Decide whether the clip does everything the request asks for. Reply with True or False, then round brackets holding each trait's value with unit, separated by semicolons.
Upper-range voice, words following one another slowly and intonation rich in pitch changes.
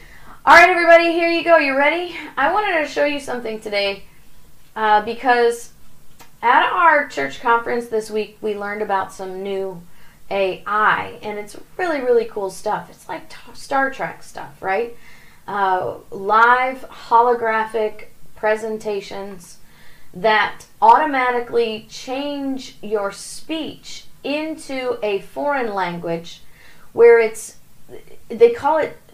True (230 Hz; 120 wpm; 6.2 semitones)